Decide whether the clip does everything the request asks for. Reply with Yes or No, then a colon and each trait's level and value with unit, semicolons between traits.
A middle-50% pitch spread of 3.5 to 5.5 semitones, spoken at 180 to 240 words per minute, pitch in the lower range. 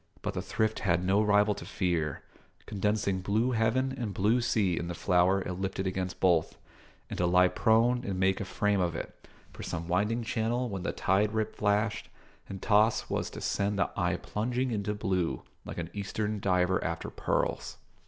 No: average, 3.1 semitones; average, 185 wpm; low, 100 Hz